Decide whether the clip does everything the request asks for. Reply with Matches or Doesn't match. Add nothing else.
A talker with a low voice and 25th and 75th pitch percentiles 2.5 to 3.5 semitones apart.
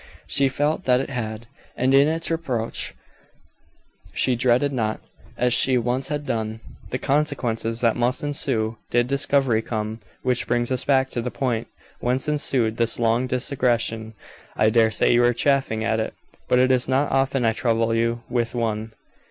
Matches